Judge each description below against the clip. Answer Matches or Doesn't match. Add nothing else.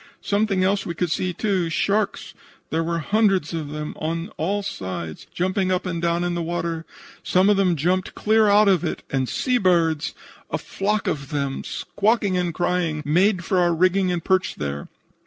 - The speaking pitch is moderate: Matches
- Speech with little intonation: Doesn't match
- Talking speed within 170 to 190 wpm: Matches